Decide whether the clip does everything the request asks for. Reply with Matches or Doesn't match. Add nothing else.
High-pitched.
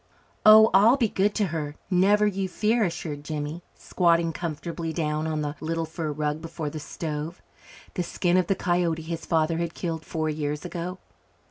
Doesn't match